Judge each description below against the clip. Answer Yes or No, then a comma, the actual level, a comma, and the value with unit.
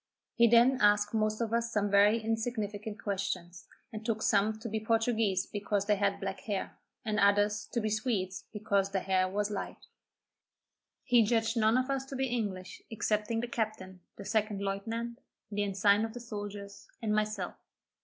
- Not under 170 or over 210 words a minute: Yes, average, 175 wpm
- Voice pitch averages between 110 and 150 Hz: No, high, 210 Hz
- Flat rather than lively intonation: Yes, narrow, 2.1 semitones